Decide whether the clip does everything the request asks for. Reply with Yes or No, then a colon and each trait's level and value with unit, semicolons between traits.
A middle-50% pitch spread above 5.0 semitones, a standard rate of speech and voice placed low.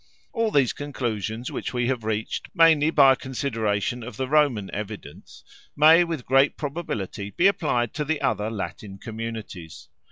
Yes: wide, 5.4 semitones; average, 155 wpm; low, 125 Hz